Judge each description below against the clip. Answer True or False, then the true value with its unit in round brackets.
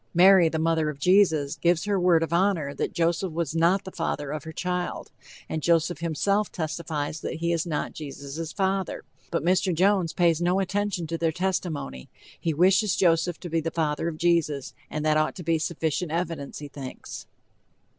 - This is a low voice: False (165 Hz)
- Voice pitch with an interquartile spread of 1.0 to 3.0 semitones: True (2.5 semitones)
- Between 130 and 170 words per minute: False (185 wpm)